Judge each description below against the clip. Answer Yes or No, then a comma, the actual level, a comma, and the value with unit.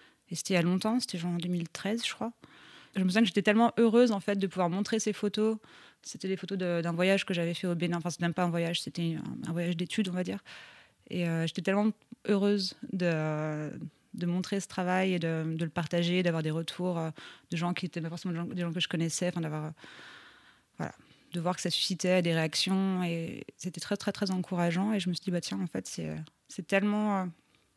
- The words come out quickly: Yes, fast, 235 wpm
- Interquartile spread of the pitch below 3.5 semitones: Yes, average, 2.9 semitones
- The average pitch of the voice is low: No, medium, 180 Hz